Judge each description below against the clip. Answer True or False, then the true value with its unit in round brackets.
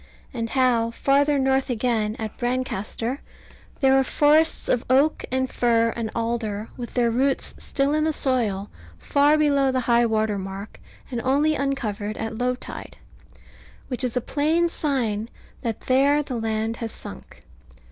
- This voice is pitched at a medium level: False (250 Hz)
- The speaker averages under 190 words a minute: True (150 wpm)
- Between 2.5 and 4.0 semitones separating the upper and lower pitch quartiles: True (3.4 semitones)